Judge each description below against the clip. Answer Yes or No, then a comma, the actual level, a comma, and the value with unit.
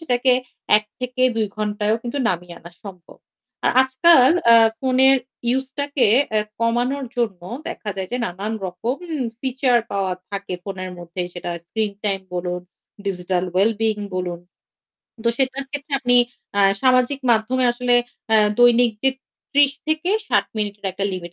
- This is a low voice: No, high, 230 Hz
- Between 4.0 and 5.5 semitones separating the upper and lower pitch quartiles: Yes, average, 5.1 semitones